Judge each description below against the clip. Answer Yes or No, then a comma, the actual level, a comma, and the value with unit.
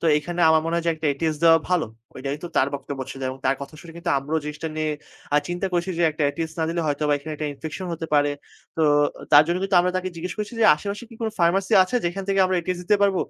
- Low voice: No, medium, 165 Hz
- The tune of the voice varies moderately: Yes, average, 3.3 semitones